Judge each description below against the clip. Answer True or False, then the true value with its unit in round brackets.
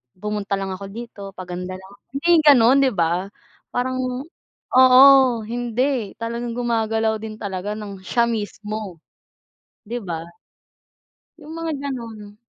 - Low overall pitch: False (220 Hz)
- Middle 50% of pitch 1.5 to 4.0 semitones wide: True (3.6 semitones)